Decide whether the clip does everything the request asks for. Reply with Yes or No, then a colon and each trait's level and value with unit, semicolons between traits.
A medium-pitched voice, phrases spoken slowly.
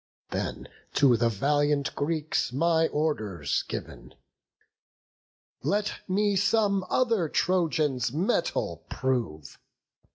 Yes: medium, 150 Hz; slow, 90 wpm